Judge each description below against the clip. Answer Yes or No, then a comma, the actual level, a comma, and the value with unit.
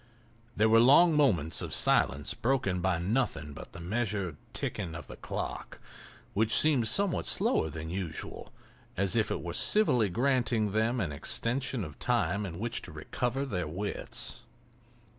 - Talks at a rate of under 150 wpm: No, average, 155 wpm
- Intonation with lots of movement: Yes, wide, 6.1 semitones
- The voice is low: Yes, low, 105 Hz